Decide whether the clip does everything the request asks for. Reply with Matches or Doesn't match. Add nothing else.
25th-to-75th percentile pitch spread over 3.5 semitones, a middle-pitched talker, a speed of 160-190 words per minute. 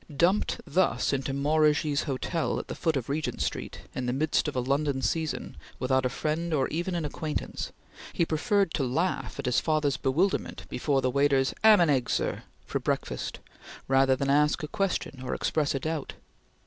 Doesn't match